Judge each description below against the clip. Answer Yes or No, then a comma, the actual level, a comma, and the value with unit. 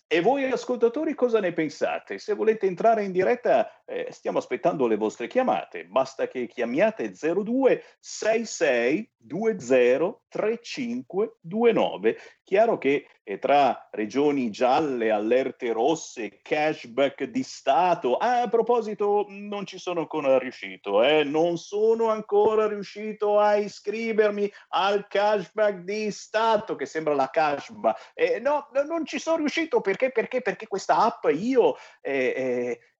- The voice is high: Yes, high, 215 Hz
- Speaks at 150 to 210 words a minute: No, average, 135 wpm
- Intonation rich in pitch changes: Yes, wide, 6.4 semitones